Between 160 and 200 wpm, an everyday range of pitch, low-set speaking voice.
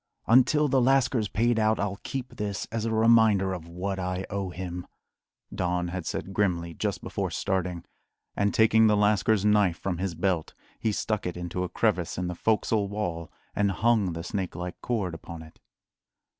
Yes: average, 180 wpm; average, 3.7 semitones; low, 100 Hz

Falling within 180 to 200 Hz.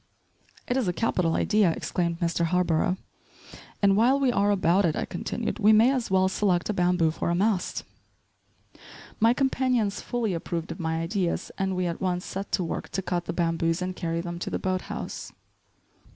Yes: medium, 185 Hz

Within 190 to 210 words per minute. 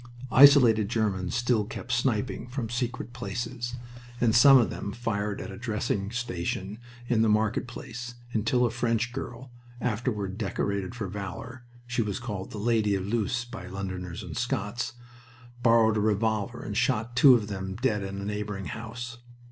No: average, 165 wpm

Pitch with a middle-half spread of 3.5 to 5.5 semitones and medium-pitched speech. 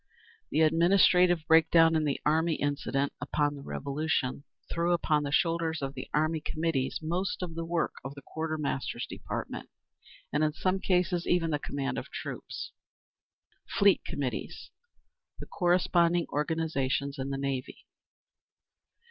No: average, 3.1 semitones; medium, 155 Hz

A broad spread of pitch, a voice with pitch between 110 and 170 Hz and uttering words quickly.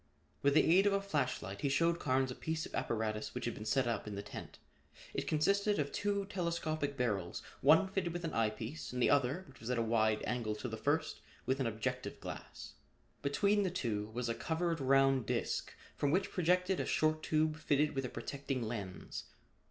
Yes: wide, 6.1 semitones; medium, 140 Hz; fast, 210 wpm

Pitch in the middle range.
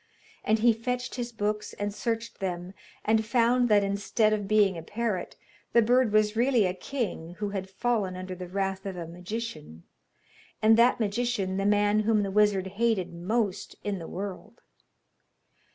No: high, 205 Hz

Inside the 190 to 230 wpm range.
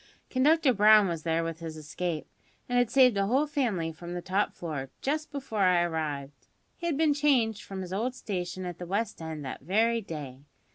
Yes: average, 200 wpm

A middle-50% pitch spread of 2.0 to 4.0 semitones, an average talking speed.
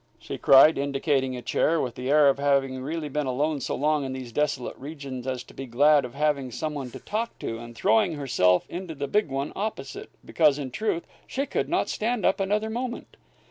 No: average, 3.6 semitones; fast, 215 wpm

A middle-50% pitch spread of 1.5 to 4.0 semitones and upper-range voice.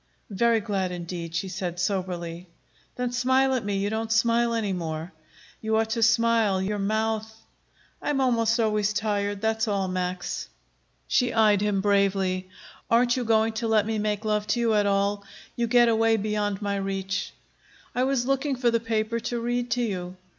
Yes: average, 2.9 semitones; high, 215 Hz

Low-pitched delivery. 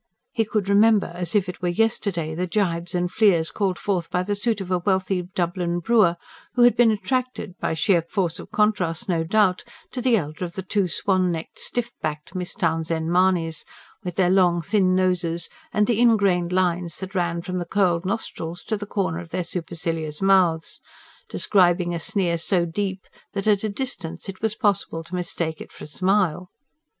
No: medium, 180 Hz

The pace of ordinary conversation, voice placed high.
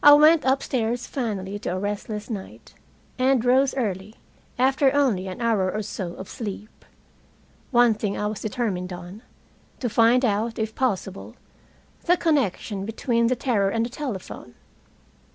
Yes: average, 150 wpm; high, 225 Hz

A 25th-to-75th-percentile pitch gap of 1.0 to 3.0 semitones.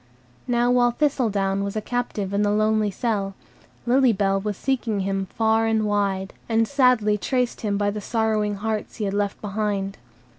Yes: narrow, 2.6 semitones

